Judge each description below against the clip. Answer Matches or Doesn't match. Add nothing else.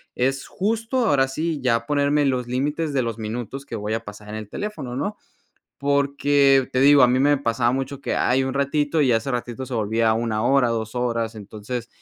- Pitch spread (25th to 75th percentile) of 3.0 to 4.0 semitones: Matches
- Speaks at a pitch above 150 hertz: Doesn't match